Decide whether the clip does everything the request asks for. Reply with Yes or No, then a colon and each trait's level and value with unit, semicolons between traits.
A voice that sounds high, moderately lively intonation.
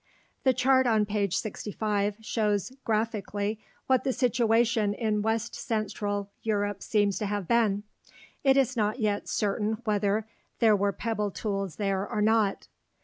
No: high, 210 Hz; narrow, 1.9 semitones